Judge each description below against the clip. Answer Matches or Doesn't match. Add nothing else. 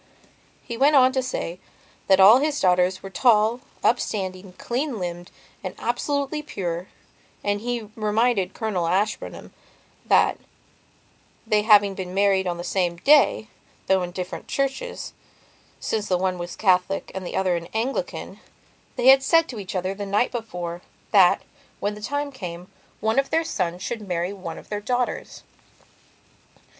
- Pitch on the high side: Matches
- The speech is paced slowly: Doesn't match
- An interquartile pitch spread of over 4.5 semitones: Matches